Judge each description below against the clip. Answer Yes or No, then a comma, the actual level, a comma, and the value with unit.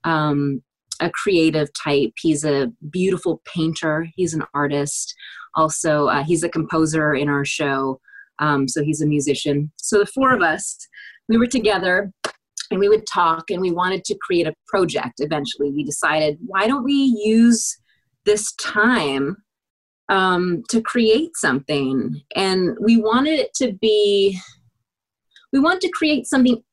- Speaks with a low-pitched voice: No, medium, 175 Hz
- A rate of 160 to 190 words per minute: No, average, 150 wpm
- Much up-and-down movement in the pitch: Yes, wide, 7.0 semitones